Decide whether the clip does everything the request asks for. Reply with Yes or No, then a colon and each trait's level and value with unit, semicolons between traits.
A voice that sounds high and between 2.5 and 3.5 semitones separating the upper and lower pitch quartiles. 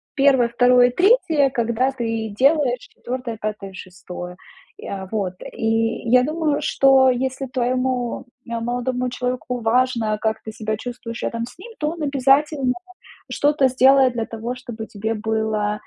Yes: high, 245 Hz; average, 2.9 semitones